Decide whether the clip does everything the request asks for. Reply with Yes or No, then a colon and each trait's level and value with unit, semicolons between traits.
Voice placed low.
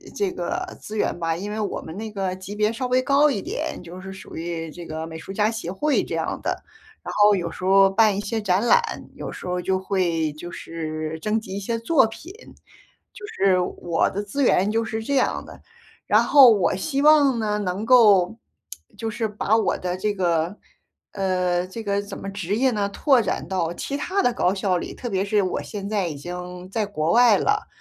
No: high, 200 Hz